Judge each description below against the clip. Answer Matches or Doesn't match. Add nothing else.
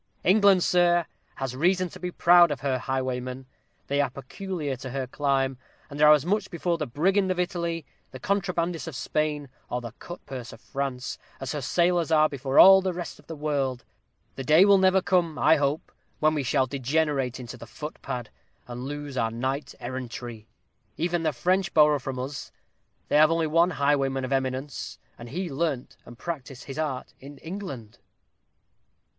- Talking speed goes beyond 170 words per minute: Matches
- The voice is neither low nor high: Matches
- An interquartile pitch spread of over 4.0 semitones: Matches